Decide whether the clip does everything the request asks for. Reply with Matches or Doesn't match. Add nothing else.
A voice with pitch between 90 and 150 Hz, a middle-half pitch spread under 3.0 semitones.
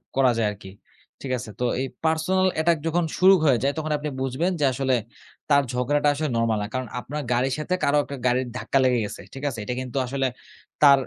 Doesn't match